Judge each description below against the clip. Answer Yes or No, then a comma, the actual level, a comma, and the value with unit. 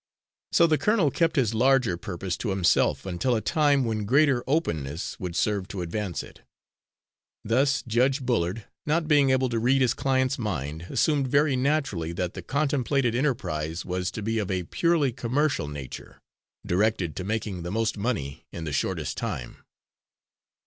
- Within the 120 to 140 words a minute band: No, average, 165 wpm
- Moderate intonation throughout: No, wide, 7.1 semitones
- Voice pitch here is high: No, low, 115 Hz